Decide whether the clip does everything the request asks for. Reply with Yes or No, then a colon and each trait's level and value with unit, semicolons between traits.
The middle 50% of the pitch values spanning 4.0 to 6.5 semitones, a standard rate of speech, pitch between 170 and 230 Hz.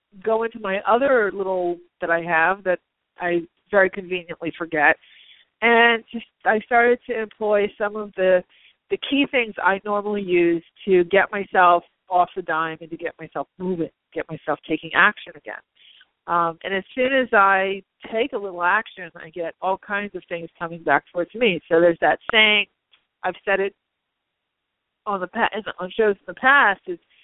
No: average, 3.6 semitones; average, 175 wpm; high, 190 Hz